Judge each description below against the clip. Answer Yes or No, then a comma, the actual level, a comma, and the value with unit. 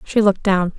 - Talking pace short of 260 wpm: Yes, fast, 230 wpm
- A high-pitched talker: Yes, high, 195 Hz